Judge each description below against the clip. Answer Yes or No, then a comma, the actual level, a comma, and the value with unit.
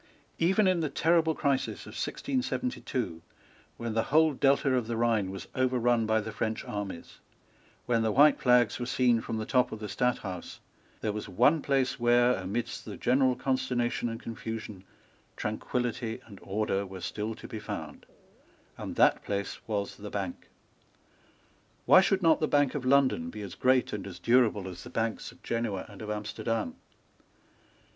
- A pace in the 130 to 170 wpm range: Yes, average, 165 wpm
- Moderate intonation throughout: Yes, average, 3.6 semitones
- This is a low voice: Yes, low, 115 Hz